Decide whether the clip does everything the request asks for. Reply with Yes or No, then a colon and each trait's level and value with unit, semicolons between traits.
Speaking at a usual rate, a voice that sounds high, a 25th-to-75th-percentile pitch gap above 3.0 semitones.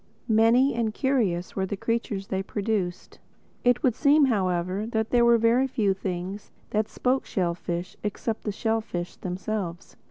Yes: average, 150 wpm; high, 215 Hz; average, 4.0 semitones